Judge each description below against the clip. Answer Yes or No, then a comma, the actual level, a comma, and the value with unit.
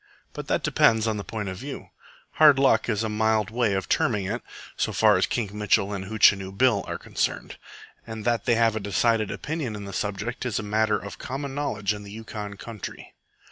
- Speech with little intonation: Yes, narrow, 2.3 semitones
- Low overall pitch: Yes, low, 110 Hz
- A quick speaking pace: Yes, fast, 210 wpm